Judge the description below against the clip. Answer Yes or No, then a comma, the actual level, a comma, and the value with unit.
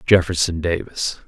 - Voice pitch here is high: No, very low, 85 Hz